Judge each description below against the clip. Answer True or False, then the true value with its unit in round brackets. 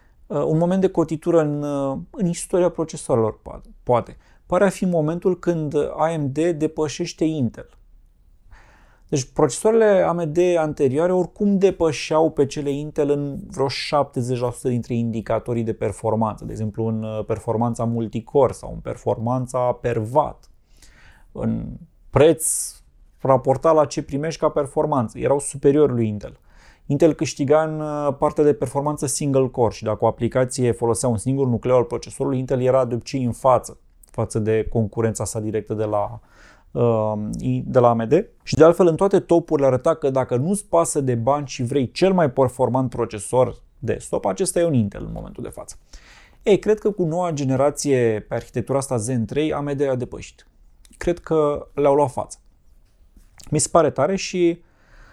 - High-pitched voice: False (135 Hz)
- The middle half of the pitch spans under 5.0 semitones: False (5.4 semitones)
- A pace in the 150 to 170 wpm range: True (155 wpm)